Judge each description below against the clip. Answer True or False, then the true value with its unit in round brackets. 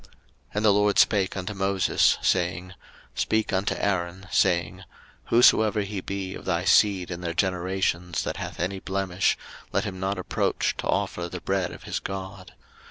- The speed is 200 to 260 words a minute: False (170 wpm)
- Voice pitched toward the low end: True (95 Hz)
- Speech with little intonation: True (1.6 semitones)